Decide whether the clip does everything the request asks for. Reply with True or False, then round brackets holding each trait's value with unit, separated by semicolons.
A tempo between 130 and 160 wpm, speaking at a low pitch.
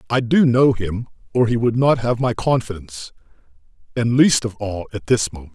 False (195 wpm; 115 Hz)